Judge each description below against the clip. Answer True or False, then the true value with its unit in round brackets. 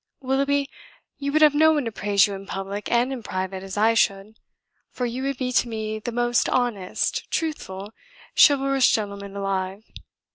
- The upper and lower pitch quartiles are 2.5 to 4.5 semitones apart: False (5.2 semitones)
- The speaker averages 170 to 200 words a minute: True (175 wpm)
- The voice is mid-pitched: False (225 Hz)